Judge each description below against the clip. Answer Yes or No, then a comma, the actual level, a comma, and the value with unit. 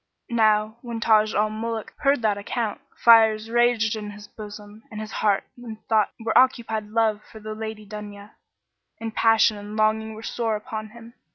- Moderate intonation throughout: No, narrow, 1.2 semitones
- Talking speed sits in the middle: Yes, average, 175 wpm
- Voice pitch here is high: Yes, high, 220 Hz